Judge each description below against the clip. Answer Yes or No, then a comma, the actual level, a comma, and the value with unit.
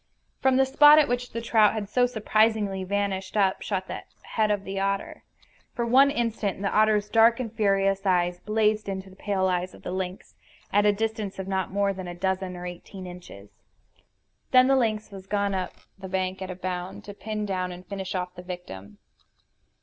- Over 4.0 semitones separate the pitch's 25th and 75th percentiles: No, narrow, 2.6 semitones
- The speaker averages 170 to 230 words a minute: Yes, average, 200 wpm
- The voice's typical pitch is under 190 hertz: No, high, 195 Hz